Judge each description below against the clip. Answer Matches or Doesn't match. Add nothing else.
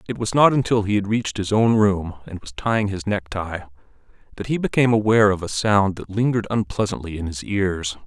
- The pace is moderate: Doesn't match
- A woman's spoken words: Doesn't match